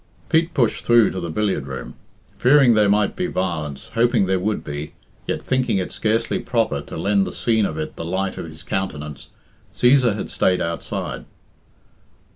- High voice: No, low, 100 Hz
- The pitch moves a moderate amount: No, wide, 6.0 semitones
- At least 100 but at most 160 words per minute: No, average, 175 wpm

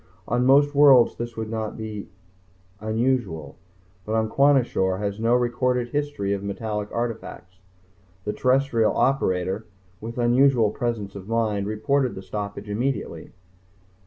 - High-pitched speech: No, low, 115 Hz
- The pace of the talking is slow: Yes, slow, 125 wpm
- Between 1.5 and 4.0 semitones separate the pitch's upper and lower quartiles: Yes, average, 3.6 semitones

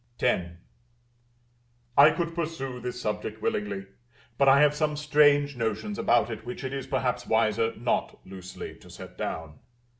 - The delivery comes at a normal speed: Yes, average, 150 wpm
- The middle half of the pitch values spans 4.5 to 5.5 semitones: Yes, average, 5.1 semitones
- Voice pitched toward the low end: Yes, low, 125 Hz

